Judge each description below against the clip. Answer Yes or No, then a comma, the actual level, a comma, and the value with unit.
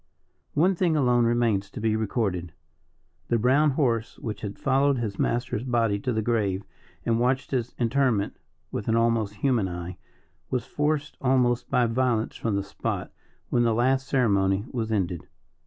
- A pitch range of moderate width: Yes, average, 3.6 semitones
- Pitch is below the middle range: Yes, low, 115 Hz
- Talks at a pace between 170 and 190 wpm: No, average, 160 wpm